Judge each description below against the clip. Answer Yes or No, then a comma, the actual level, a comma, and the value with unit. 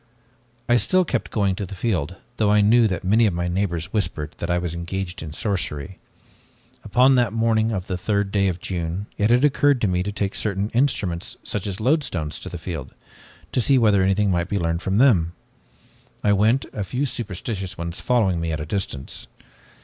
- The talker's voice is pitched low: Yes, low, 100 Hz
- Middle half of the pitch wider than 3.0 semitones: Yes, average, 4.3 semitones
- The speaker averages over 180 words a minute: Yes, average, 200 wpm